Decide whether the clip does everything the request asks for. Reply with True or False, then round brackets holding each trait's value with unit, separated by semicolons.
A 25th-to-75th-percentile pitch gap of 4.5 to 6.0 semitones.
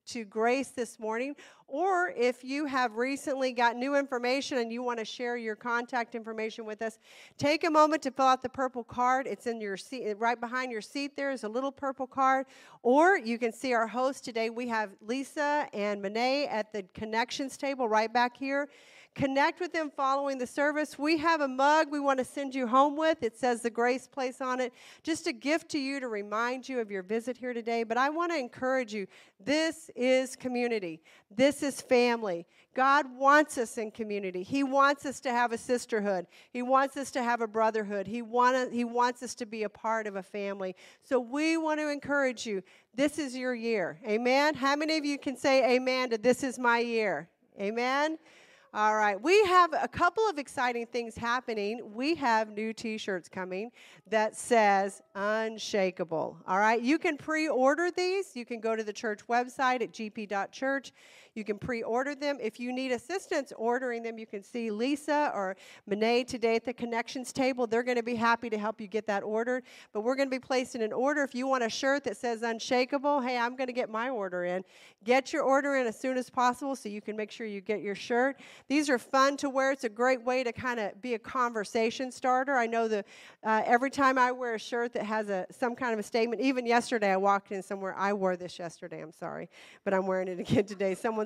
False (3.6 semitones)